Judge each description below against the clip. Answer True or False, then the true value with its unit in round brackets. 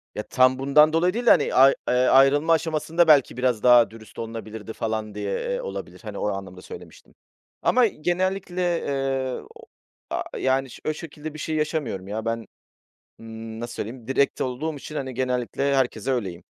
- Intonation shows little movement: False (5.2 semitones)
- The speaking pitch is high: False (130 Hz)